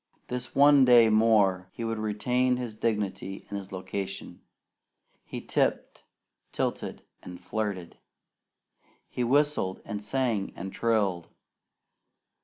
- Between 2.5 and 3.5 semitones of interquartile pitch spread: No, average, 4.0 semitones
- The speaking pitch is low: Yes, low, 110 Hz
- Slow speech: Yes, slow, 110 wpm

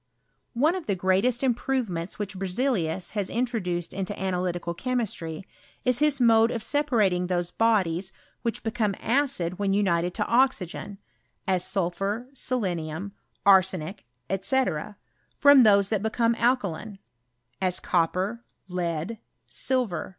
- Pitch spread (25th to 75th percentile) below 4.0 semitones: No, average, 4.8 semitones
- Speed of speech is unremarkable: No, slow, 115 wpm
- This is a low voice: No, high, 200 Hz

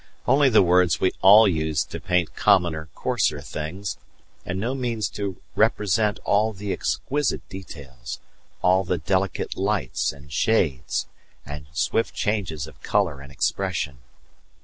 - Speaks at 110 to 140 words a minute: Yes, slow, 135 wpm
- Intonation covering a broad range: No, average, 4.9 semitones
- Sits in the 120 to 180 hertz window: No, very low, 95 Hz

